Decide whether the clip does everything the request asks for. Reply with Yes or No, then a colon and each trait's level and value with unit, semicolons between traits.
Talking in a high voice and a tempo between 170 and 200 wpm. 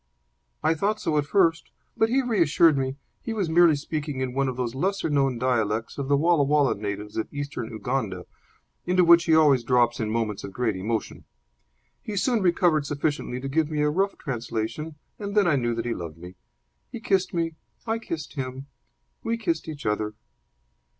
No: medium, 145 Hz; average, 190 wpm